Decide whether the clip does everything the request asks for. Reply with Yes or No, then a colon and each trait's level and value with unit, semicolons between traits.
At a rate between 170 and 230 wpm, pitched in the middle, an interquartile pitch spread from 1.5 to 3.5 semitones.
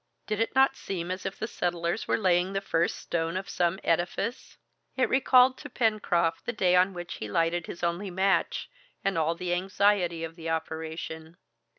Yes: average, 185 wpm; medium, 180 Hz; average, 2.9 semitones